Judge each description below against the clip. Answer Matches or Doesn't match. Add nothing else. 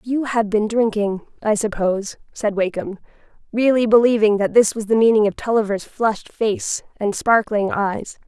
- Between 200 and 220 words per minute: Doesn't match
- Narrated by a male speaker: Doesn't match